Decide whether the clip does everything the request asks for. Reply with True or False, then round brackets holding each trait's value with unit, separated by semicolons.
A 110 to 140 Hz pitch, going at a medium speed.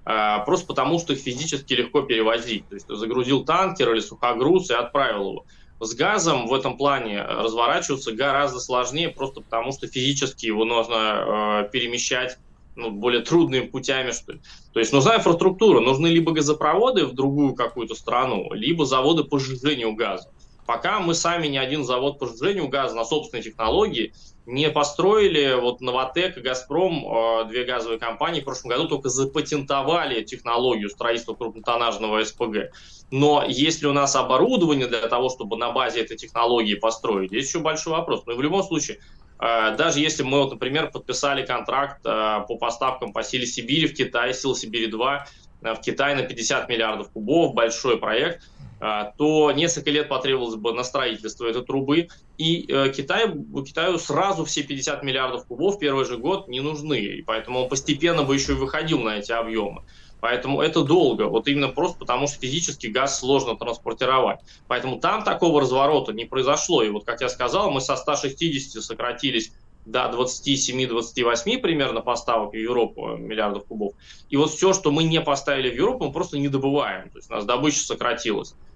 False (135 Hz; 165 wpm)